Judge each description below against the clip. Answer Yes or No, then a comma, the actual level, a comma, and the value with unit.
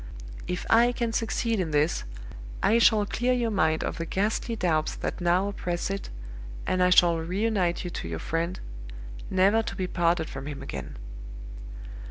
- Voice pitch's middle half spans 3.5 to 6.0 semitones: Yes, average, 4.5 semitones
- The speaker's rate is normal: Yes, average, 170 wpm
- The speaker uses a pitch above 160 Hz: Yes, medium, 185 Hz